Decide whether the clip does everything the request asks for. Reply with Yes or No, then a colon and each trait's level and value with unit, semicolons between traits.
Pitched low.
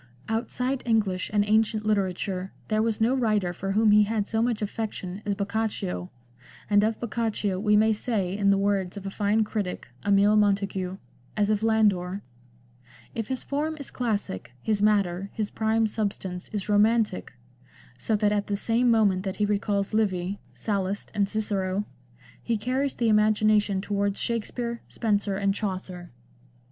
No: high, 210 Hz